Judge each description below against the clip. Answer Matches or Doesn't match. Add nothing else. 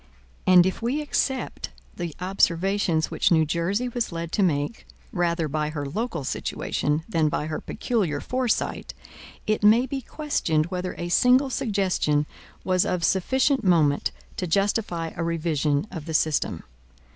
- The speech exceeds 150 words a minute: Doesn't match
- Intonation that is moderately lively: Doesn't match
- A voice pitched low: Doesn't match